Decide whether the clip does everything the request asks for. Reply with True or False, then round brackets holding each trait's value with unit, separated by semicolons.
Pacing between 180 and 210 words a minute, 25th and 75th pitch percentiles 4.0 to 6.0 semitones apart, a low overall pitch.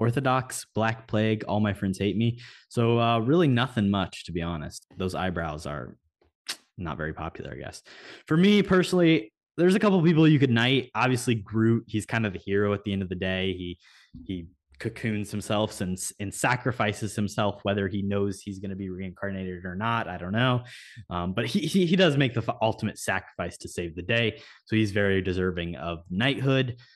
True (195 wpm; 4.4 semitones; 105 Hz)